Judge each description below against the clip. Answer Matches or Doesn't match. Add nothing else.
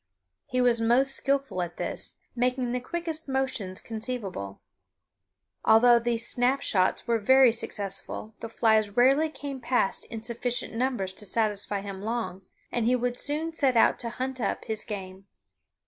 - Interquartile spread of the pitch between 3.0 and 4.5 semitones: Matches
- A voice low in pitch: Doesn't match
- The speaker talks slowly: Doesn't match